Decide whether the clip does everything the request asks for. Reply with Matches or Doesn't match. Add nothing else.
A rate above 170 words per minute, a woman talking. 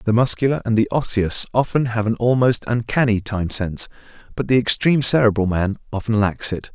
Doesn't match